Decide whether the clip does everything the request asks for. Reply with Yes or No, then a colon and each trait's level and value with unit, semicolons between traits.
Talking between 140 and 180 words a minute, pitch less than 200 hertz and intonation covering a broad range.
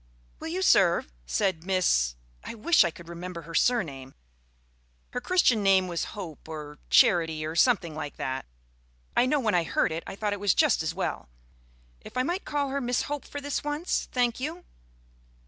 No: average, 190 wpm; high, 190 Hz; wide, 7.9 semitones